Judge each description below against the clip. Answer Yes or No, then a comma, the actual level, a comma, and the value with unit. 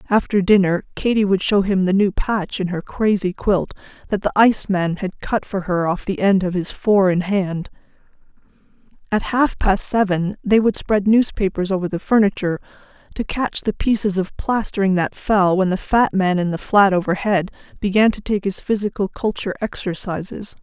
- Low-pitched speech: No, high, 195 Hz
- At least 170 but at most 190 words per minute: Yes, average, 180 wpm